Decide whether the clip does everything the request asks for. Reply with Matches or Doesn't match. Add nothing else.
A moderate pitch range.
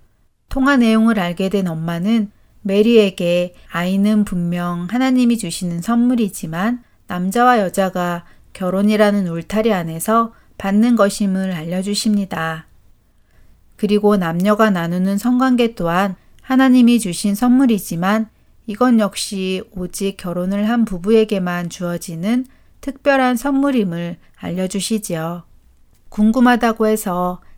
Matches